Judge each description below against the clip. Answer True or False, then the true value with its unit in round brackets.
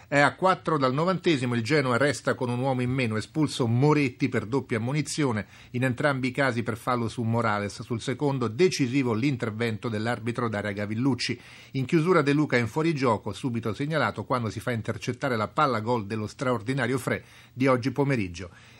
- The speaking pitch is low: True (125 Hz)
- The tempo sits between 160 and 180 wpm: True (170 wpm)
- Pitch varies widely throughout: False (3.2 semitones)